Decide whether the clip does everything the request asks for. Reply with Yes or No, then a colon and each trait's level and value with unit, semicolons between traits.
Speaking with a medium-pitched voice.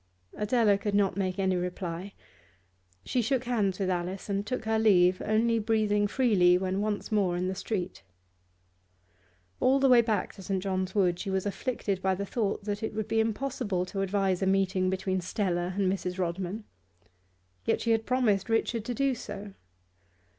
No: high, 200 Hz